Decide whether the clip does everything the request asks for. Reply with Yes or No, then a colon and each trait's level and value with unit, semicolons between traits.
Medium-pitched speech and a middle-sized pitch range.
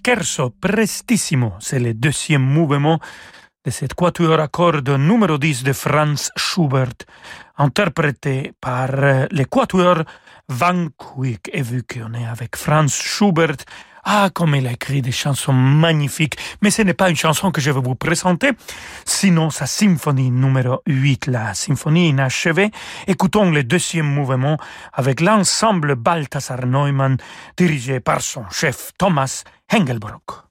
Yes: medium, 150 Hz; average, 4.6 semitones